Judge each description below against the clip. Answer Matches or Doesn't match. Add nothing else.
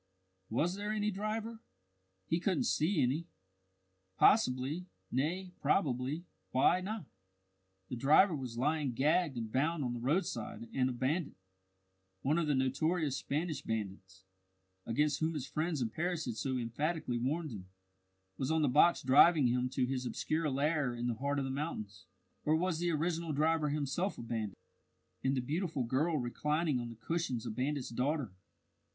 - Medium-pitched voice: Matches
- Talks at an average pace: Matches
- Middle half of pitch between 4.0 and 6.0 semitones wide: Matches